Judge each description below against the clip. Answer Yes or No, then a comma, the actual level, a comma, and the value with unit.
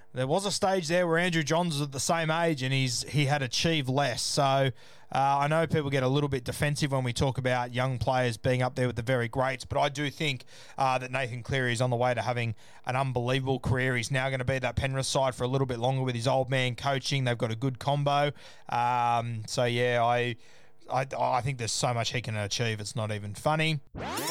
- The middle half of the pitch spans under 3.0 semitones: Yes, narrow, 2.5 semitones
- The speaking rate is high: Yes, fast, 245 wpm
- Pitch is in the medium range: No, low, 130 Hz